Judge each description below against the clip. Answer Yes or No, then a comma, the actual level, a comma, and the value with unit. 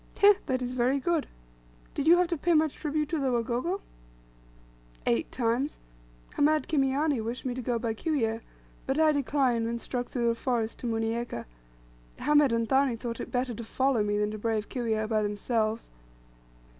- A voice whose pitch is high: Yes, high, 245 Hz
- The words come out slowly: No, average, 175 wpm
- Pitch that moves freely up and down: No, average, 4.0 semitones